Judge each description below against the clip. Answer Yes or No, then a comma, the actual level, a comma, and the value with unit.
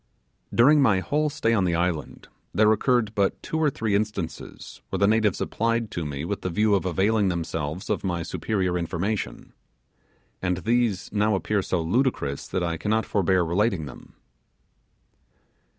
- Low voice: Yes, low, 100 Hz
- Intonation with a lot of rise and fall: No, average, 4.1 semitones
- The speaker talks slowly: No, average, 160 wpm